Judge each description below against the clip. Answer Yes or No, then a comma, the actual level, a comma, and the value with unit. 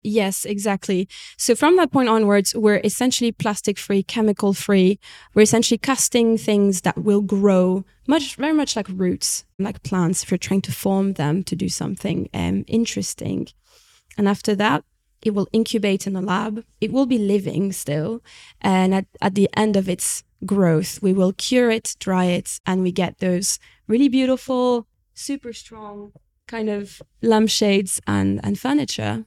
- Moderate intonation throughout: Yes, average, 3.4 semitones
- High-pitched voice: Yes, high, 205 Hz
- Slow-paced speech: No, average, 165 wpm